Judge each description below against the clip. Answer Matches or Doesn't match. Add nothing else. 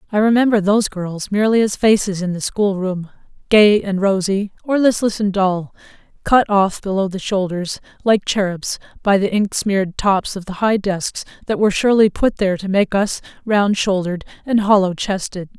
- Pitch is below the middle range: Doesn't match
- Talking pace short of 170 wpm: Doesn't match